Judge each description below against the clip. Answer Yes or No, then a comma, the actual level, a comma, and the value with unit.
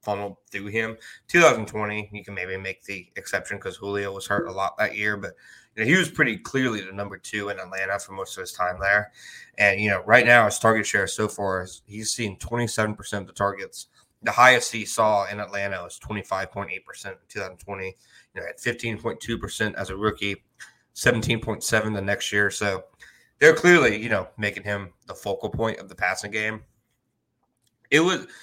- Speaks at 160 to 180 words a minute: No, average, 195 wpm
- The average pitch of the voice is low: Yes, low, 105 Hz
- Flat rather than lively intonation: Yes, narrow, 1.8 semitones